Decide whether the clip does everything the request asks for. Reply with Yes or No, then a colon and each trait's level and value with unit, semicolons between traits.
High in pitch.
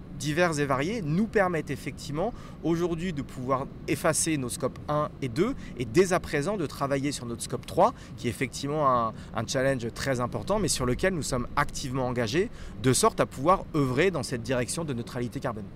No: medium, 140 Hz